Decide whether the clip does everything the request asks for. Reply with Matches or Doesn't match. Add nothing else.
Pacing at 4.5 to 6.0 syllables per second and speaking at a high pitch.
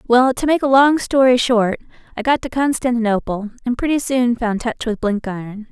Matches